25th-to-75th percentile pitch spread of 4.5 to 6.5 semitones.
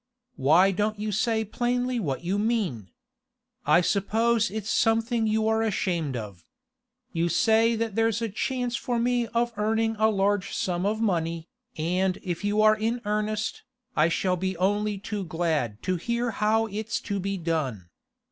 No: average, 4.0 semitones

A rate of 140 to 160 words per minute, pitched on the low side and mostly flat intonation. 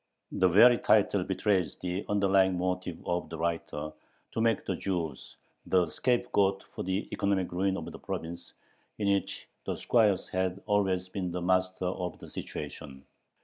Yes: average, 155 wpm; very low, 95 Hz; narrow, 1.9 semitones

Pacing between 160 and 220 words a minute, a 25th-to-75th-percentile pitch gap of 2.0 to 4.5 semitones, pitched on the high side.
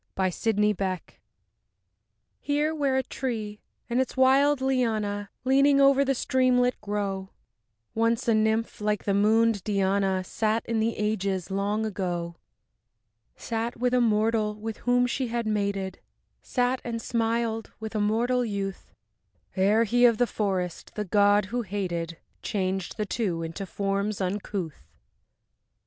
No: average, 140 wpm; average, 3.3 semitones; high, 215 Hz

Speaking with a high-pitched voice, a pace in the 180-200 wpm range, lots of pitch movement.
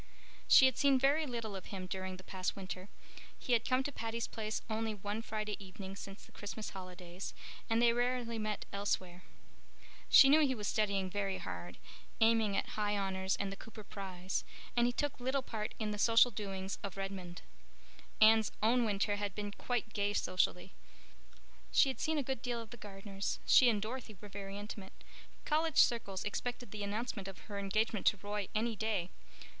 No: high, 210 Hz; average, 185 wpm; average, 3.1 semitones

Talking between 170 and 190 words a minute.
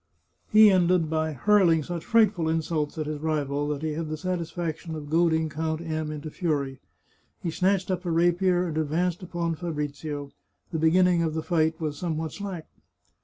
Yes: average, 175 wpm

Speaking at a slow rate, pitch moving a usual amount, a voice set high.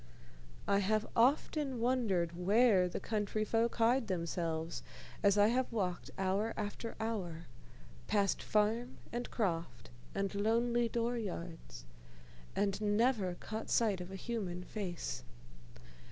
Yes: slow, 120 wpm; average, 4.2 semitones; high, 210 Hz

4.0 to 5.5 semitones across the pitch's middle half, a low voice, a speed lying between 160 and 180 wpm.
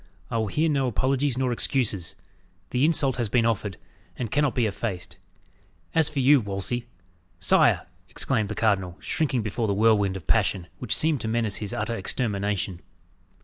Yes: average, 4.4 semitones; low, 115 Hz; average, 170 wpm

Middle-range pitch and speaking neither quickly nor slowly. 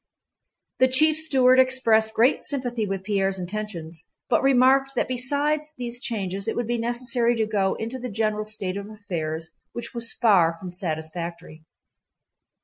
No: high, 220 Hz; average, 150 wpm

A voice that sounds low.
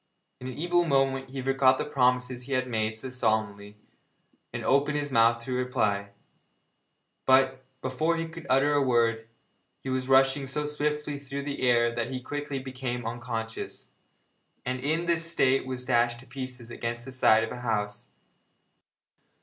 Yes: low, 130 Hz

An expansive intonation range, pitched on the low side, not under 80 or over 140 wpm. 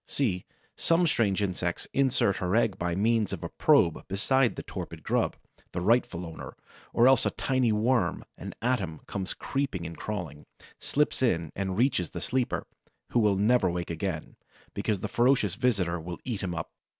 No: wide, 5.8 semitones; low, 100 Hz; average, 175 wpm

